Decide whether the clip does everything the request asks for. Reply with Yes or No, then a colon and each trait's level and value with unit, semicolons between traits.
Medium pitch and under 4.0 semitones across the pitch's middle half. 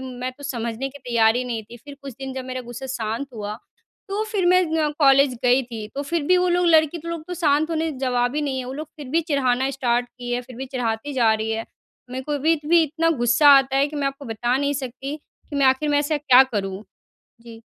No: very high, 265 Hz; average, 3.3 semitones